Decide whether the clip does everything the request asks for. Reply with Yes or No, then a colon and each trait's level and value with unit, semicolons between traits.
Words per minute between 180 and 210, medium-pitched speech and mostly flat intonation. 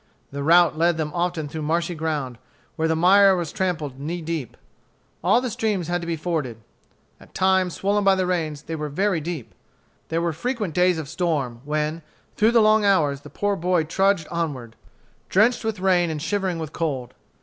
No: average, 190 wpm; medium, 170 Hz; average, 3.7 semitones